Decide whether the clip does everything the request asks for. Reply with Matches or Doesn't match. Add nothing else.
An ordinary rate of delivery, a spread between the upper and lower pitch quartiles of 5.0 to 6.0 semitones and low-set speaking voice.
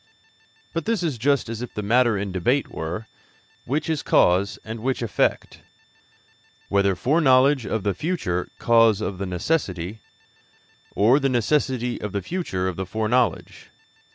Matches